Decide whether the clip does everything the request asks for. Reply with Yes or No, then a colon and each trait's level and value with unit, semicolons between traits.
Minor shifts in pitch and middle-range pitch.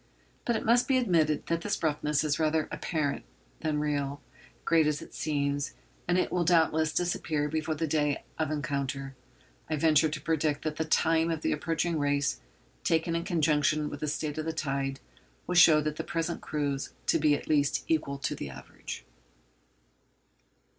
Yes: narrow, 2.0 semitones; medium, 155 Hz